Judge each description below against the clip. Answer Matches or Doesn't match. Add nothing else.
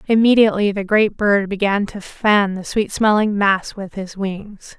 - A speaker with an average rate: Matches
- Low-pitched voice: Doesn't match